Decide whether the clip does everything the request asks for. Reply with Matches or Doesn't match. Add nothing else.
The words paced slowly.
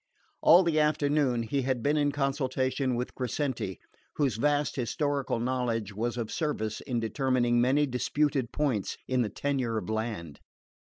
Doesn't match